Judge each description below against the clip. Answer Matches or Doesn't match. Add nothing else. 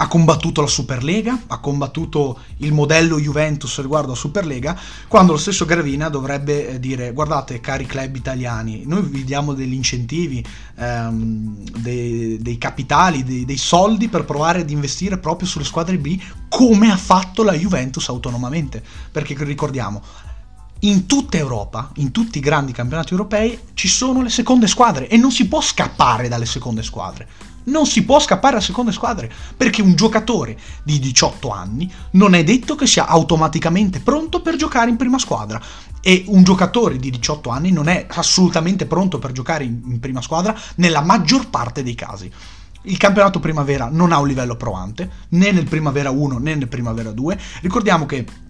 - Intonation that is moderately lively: Doesn't match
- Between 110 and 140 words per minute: Doesn't match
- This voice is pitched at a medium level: Matches